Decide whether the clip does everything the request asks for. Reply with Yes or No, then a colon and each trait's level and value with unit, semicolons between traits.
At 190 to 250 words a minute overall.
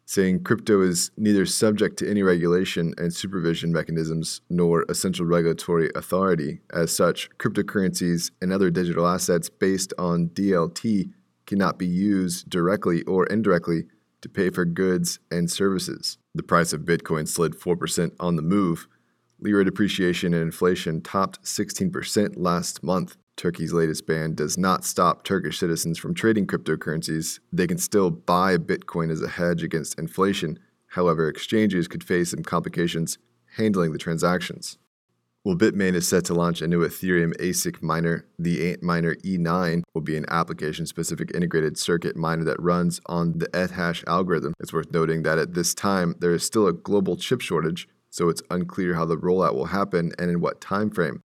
No: average, 165 wpm